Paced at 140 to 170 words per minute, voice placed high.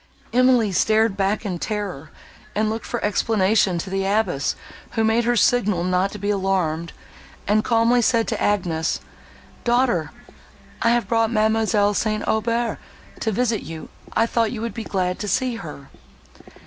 Yes: average, 160 wpm; high, 215 Hz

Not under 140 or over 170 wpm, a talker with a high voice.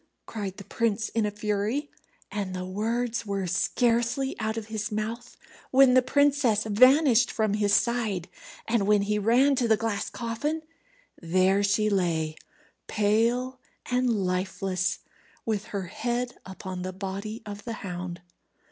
Yes: average, 145 wpm; high, 215 Hz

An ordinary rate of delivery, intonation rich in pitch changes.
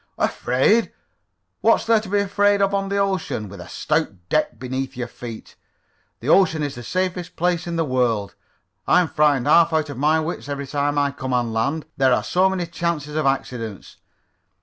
Yes: average, 190 wpm; wide, 5.8 semitones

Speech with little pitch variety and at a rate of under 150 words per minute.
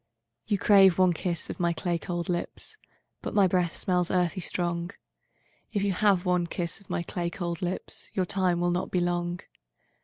No: narrow, 1.5 semitones; average, 165 wpm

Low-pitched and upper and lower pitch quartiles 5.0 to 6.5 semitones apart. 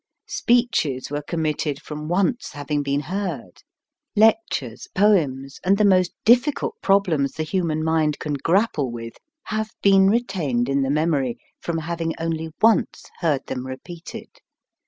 No: medium, 160 Hz; wide, 5.6 semitones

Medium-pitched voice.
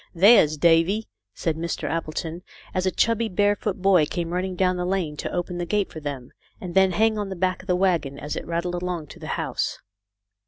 Yes: medium, 180 Hz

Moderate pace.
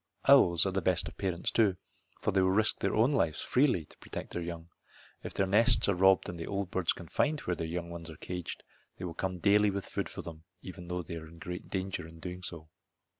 No: fast, 240 wpm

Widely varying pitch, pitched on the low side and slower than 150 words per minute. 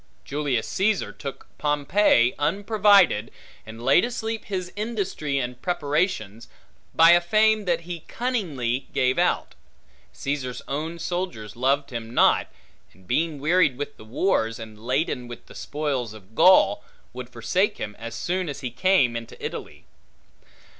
No: wide, 7.1 semitones; medium, 145 Hz; average, 140 wpm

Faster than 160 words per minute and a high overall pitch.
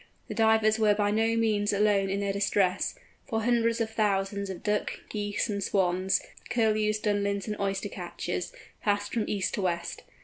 Yes: average, 170 wpm; high, 205 Hz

